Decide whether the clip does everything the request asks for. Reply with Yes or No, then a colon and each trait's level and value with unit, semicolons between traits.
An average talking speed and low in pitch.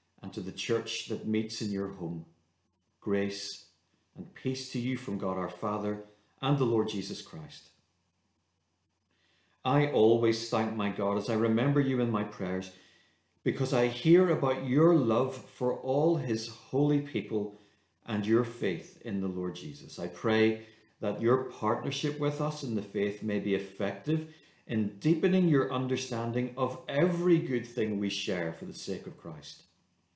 Yes: average, 160 wpm; low, 110 Hz